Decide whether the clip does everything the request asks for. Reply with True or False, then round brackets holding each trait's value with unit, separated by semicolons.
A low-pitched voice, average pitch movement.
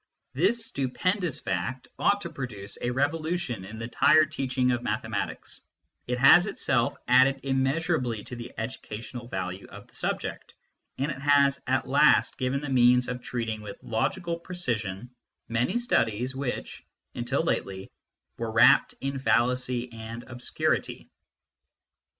True (125 Hz; 3.3 semitones)